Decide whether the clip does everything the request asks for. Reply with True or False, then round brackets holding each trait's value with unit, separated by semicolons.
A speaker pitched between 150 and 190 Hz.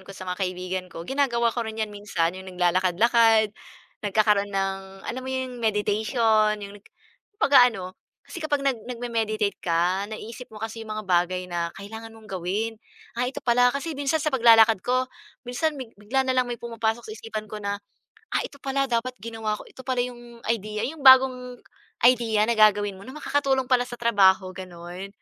False (220 Hz)